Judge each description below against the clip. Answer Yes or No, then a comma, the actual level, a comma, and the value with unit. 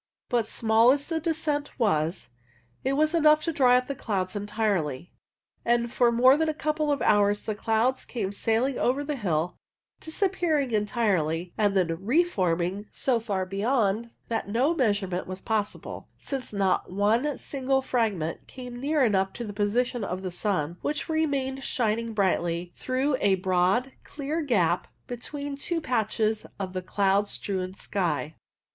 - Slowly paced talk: No, average, 150 wpm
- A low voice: No, high, 225 Hz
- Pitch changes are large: Yes, wide, 5.8 semitones